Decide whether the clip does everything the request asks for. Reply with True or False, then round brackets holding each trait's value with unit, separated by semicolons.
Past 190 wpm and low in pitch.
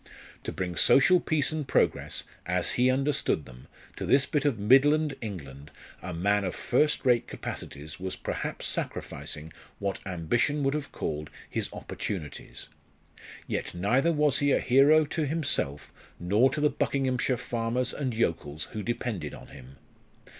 False (150 wpm; 120 Hz)